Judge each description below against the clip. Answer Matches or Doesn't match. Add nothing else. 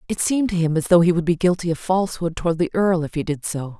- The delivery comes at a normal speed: Doesn't match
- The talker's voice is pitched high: Doesn't match